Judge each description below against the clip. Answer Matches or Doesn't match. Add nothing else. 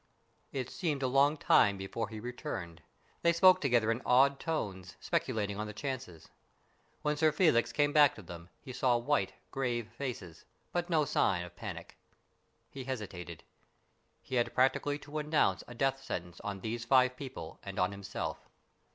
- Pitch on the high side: Doesn't match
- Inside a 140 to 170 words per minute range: Matches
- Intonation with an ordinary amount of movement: Doesn't match